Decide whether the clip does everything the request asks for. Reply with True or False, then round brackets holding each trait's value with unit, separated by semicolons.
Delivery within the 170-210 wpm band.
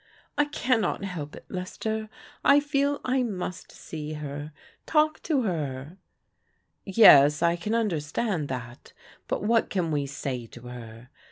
False (155 wpm)